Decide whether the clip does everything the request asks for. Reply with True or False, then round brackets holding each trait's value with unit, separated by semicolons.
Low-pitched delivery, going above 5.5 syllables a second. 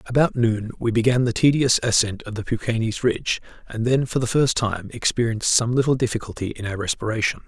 True (115 Hz; 6.0 syllables/s)